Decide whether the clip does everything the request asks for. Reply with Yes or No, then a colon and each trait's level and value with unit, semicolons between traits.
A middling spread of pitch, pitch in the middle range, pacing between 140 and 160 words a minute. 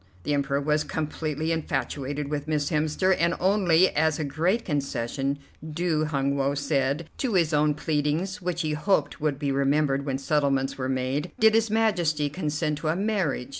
No: average, 3.0 semitones; medium, 150 Hz; average, 170 wpm